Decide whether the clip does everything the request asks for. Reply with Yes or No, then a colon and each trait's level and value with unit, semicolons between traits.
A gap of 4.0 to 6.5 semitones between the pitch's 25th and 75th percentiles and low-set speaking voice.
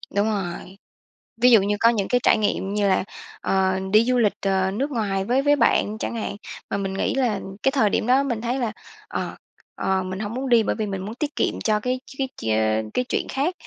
No: average, 4.4 semitones; high, 215 Hz